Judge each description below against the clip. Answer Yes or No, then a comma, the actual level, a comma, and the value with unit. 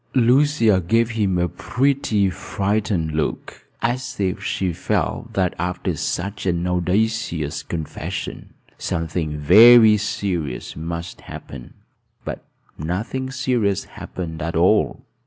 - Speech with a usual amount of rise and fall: Yes, average, 4.9 semitones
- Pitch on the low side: Yes, very low, 95 Hz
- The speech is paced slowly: Yes, slow, 110 wpm